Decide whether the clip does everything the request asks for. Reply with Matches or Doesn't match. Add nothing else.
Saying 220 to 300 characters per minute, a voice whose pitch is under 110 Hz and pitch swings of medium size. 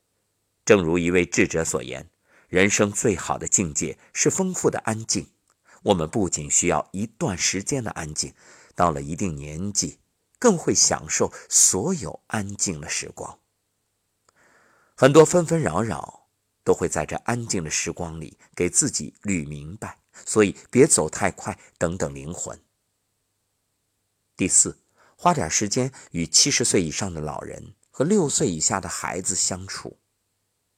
Doesn't match